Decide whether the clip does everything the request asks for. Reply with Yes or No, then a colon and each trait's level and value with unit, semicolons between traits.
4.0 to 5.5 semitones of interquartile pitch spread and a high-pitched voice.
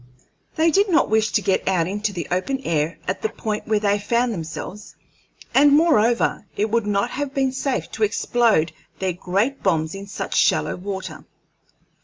Yes: average, 4.7 semitones; high, 210 Hz